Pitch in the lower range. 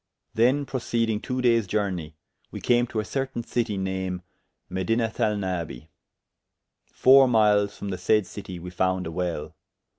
Yes: low, 105 Hz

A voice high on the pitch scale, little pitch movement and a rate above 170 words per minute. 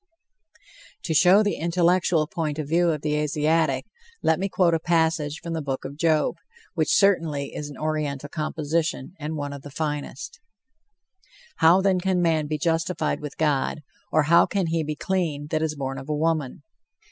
No: medium, 155 Hz; narrow, 2.2 semitones; average, 180 wpm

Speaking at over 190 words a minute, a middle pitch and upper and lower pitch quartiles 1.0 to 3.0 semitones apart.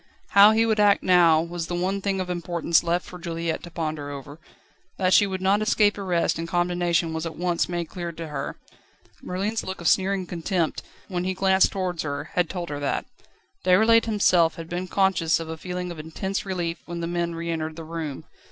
Yes: fast, 205 wpm; medium, 175 Hz; narrow, 2.4 semitones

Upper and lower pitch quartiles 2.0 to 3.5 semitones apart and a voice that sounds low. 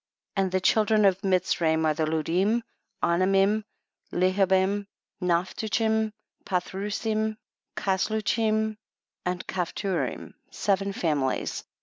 No: average, 3.1 semitones; high, 195 Hz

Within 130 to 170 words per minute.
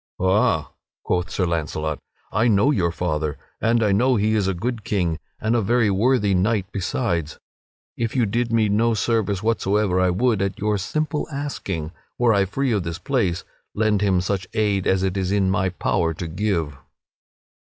No: average, 185 wpm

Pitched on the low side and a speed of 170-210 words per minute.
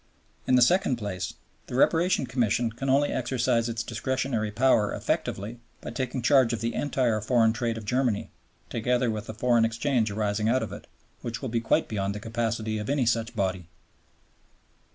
Yes: low, 115 Hz; average, 175 wpm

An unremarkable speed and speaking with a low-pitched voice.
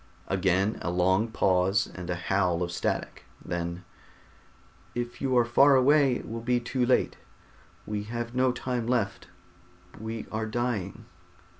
Yes: average, 145 wpm; low, 110 Hz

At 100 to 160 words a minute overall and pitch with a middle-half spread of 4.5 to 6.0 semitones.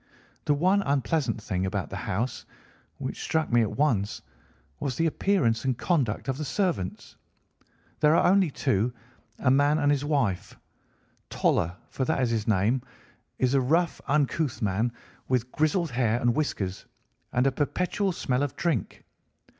Yes: average, 155 wpm; average, 5.2 semitones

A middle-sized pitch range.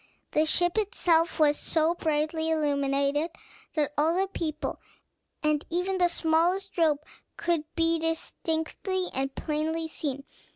No: narrow, 2.2 semitones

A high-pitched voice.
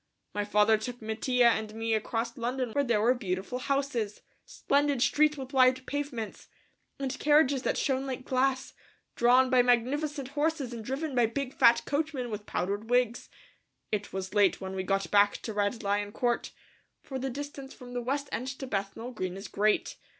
Yes: high, 245 Hz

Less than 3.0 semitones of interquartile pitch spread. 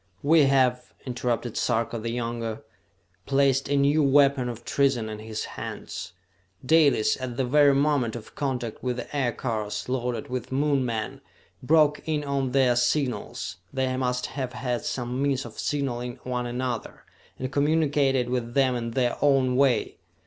Yes: narrow, 2.5 semitones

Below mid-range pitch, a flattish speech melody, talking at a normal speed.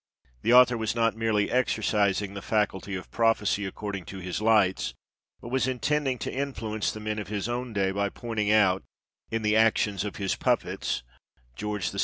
Yes: low, 105 Hz; narrow, 2.3 semitones; average, 180 wpm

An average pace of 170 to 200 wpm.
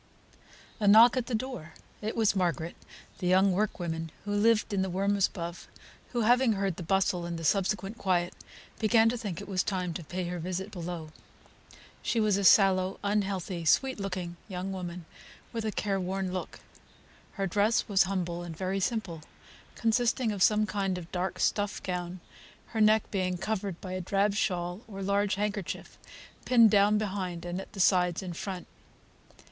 Yes: average, 175 wpm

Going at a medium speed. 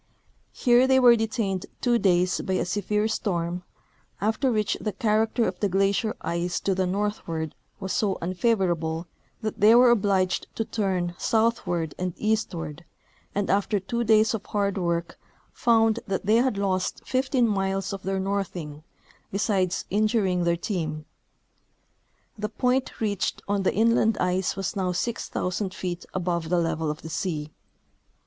Yes: average, 150 wpm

